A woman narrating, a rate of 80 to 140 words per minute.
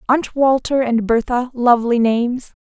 Yes: female; slow, 135 wpm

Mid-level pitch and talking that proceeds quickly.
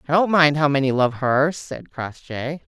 No: medium, 145 Hz; average, 195 wpm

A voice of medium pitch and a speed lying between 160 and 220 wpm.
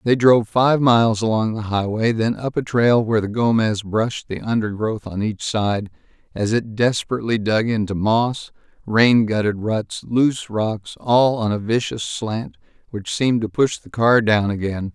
No: low, 110 Hz; average, 175 wpm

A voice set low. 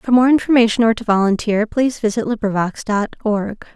No: high, 220 Hz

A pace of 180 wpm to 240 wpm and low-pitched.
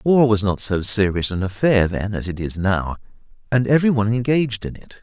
Yes: fast, 205 wpm; low, 105 Hz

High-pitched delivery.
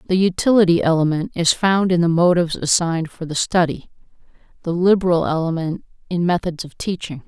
No: medium, 170 Hz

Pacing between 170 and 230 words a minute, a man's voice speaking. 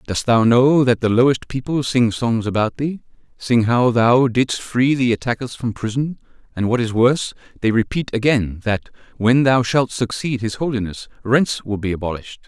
Yes: average, 180 wpm; male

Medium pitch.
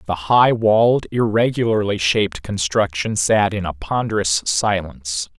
No: low, 100 Hz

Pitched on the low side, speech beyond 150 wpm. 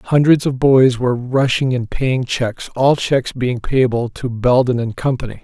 Yes: low, 125 Hz; average, 175 wpm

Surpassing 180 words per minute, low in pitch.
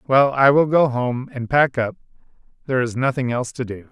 Yes: average, 200 wpm; low, 130 Hz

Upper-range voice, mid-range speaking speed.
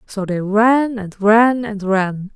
Yes: high, 210 Hz; average, 180 wpm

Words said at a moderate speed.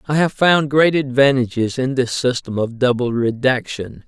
Yes: average, 160 wpm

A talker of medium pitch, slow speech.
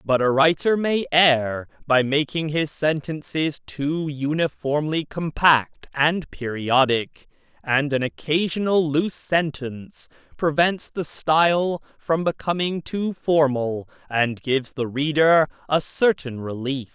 Yes: medium, 150 Hz; slow, 115 wpm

